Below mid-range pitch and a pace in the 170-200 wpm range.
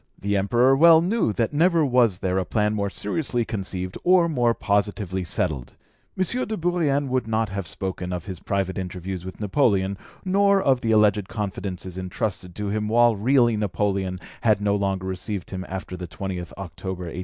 Yes: low, 100 Hz; average, 180 wpm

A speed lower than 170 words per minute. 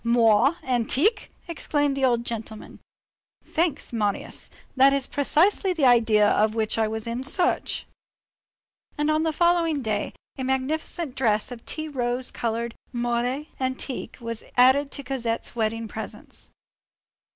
Yes: slow, 135 wpm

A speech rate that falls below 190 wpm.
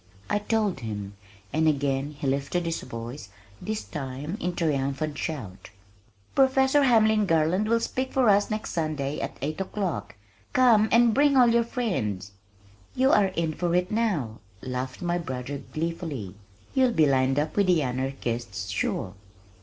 Yes: average, 155 wpm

